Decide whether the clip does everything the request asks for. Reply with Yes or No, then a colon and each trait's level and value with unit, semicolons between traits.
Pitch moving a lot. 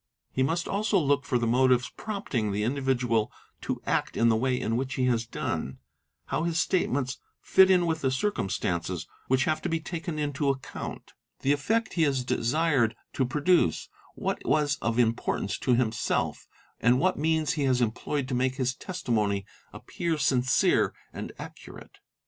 No: average, 4.8 semitones